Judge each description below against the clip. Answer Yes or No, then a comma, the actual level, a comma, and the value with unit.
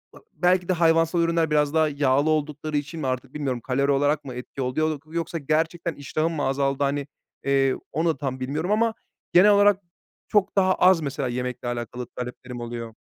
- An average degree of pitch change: Yes, average, 3.8 semitones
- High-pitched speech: No, medium, 150 Hz